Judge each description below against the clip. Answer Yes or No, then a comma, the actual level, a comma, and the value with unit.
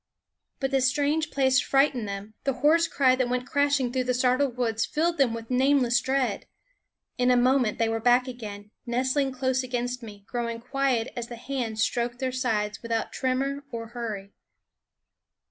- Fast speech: No, average, 170 wpm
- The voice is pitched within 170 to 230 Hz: No, very high, 250 Hz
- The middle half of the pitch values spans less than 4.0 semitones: Yes, narrow, 2.5 semitones